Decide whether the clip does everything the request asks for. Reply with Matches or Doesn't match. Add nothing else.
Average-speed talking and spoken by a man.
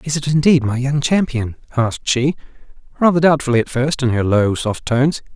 Matches